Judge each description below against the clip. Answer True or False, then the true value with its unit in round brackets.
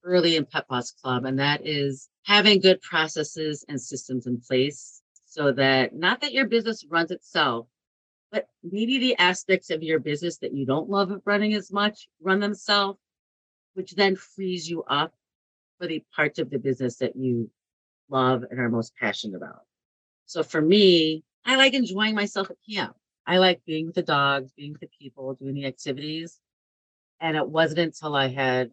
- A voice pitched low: False (155 Hz)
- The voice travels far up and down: True (6.2 semitones)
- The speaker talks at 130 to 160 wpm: False (180 wpm)